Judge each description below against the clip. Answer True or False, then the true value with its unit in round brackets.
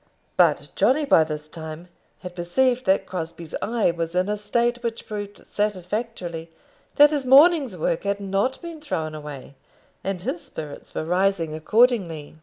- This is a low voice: False (195 Hz)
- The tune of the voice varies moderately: False (6.5 semitones)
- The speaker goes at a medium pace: True (155 wpm)